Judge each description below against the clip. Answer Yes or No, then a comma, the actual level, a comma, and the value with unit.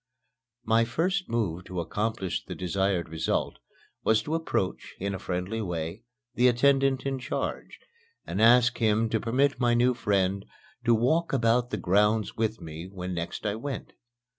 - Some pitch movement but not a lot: Yes, average, 4.5 semitones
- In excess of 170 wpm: No, average, 160 wpm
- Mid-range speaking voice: No, low, 110 Hz